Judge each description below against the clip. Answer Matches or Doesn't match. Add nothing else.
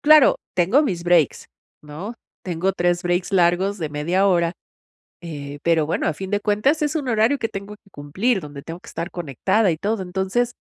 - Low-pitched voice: Doesn't match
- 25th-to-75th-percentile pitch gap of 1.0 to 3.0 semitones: Doesn't match